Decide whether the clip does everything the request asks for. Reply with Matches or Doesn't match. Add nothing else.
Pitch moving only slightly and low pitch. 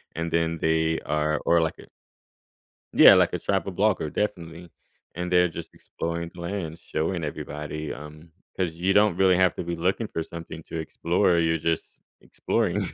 Matches